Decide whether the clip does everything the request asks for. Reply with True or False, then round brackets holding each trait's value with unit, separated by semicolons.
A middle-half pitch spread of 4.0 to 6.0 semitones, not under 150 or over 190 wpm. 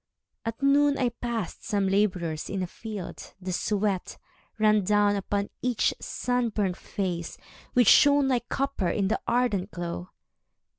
False (4.3 semitones; 140 wpm)